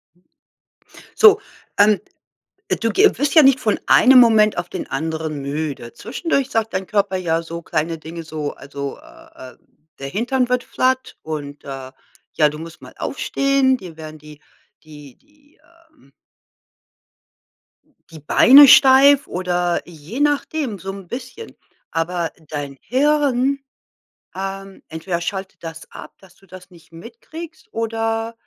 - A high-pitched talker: Yes, high, 195 Hz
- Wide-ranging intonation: Yes, wide, 8.2 semitones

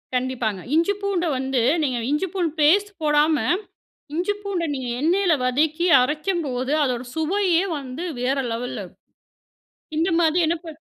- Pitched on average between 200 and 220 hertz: No, very high, 310 Hz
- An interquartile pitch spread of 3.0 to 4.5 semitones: No, average, 5.1 semitones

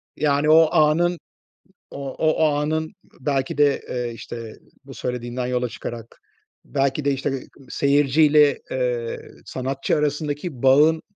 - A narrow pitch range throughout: No, average, 3.0 semitones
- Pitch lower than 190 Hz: Yes, medium, 140 Hz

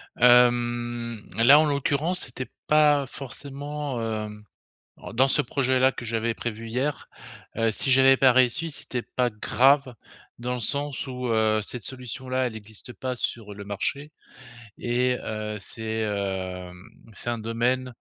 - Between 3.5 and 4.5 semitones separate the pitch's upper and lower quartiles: No, average, 3.1 semitones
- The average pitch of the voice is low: Yes, low, 120 Hz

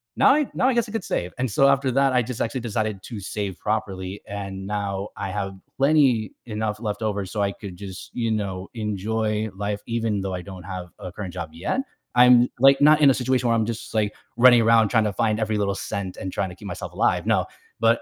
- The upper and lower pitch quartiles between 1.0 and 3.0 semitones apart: No, average, 3.4 semitones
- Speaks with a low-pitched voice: Yes, low, 110 Hz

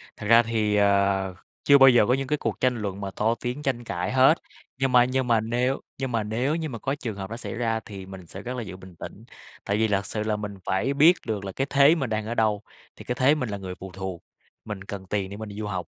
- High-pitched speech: No, low, 110 Hz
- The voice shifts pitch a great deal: No, average, 4.3 semitones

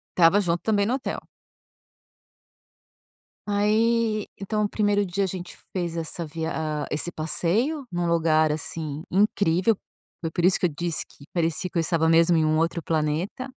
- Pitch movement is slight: No, average, 3.9 semitones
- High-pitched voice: No, medium, 175 Hz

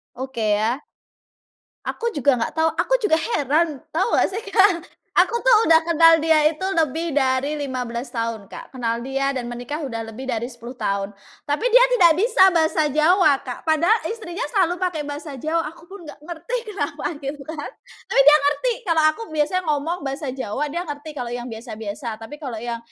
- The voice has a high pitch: Yes, very high, 295 Hz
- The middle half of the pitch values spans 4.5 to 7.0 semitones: Yes, average, 5.0 semitones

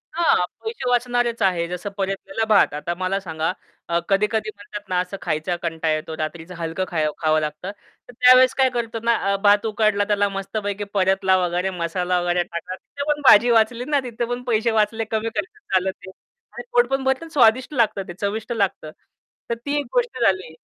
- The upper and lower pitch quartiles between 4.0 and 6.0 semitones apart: Yes, average, 4.9 semitones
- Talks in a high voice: Yes, high, 205 Hz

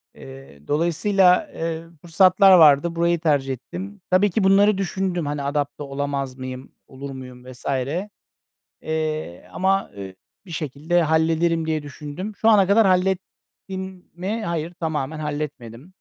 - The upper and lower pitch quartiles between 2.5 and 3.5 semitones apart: No, average, 4.7 semitones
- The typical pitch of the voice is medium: Yes, medium, 160 Hz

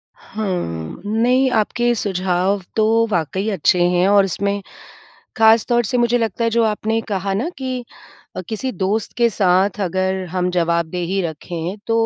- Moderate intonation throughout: Yes, average, 3.8 semitones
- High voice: Yes, high, 200 Hz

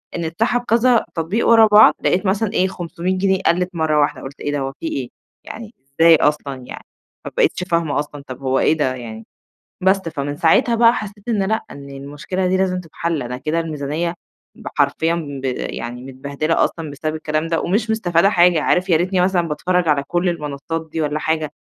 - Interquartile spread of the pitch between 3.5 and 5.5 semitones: Yes, average, 4.3 semitones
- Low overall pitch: No, medium, 165 Hz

